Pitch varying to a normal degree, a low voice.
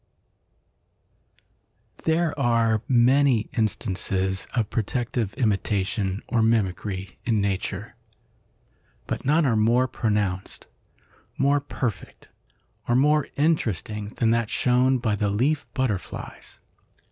Yes: average, 4.0 semitones; low, 115 Hz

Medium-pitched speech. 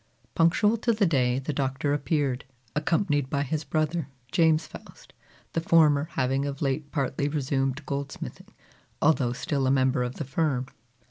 Yes: medium, 145 Hz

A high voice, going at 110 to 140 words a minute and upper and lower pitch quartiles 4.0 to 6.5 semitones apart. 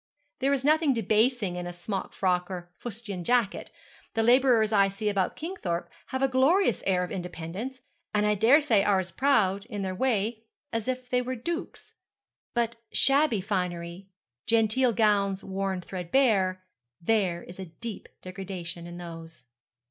No: high, 205 Hz; average, 155 wpm; average, 5.1 semitones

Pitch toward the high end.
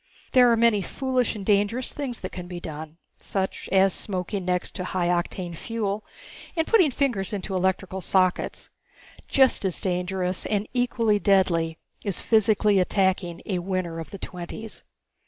Yes: high, 195 Hz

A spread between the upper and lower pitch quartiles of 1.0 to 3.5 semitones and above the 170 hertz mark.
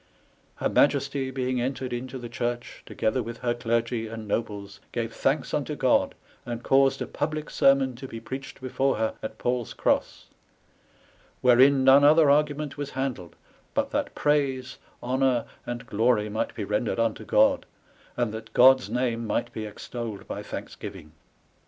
No: average, 2.8 semitones; low, 125 Hz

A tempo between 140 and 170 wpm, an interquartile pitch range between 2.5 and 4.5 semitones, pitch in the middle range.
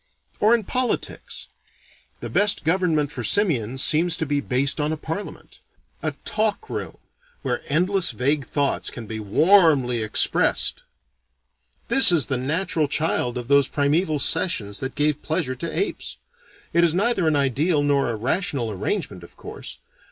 No: average, 150 wpm; average, 5.3 semitones; medium, 150 Hz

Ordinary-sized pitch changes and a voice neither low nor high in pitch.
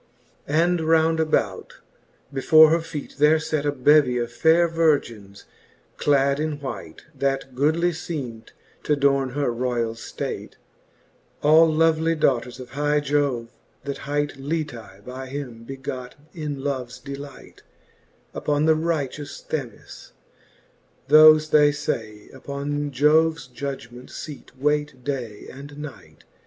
Yes: average, 3.3 semitones; medium, 145 Hz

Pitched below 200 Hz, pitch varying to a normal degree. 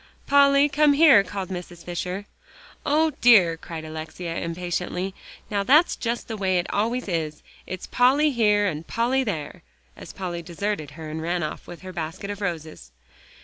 No: medium, 185 Hz; wide, 6.0 semitones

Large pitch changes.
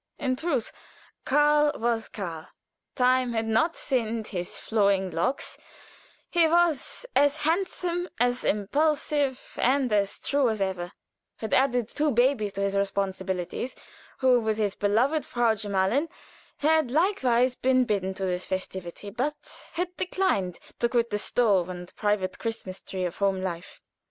Yes: wide, 6.1 semitones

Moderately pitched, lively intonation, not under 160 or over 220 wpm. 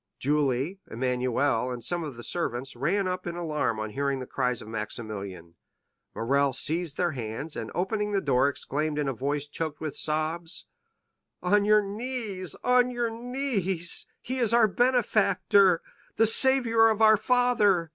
No: medium, 165 Hz; wide, 7.9 semitones; average, 145 wpm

